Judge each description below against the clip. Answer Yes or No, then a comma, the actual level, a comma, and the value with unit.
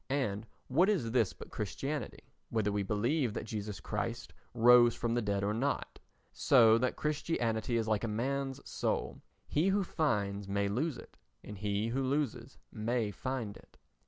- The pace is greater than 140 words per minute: Yes, average, 160 wpm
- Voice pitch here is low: Yes, low, 115 Hz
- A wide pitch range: No, average, 4.3 semitones